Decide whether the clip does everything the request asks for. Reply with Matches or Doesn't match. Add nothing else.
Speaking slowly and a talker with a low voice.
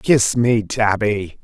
Matches